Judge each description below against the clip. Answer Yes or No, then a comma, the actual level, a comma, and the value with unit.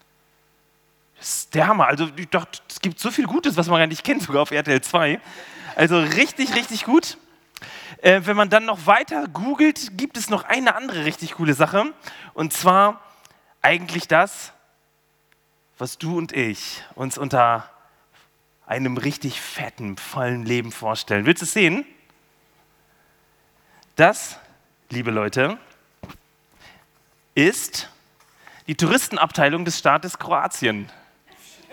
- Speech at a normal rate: No, slow, 120 wpm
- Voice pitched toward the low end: No, medium, 170 Hz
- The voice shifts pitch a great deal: Yes, wide, 6.7 semitones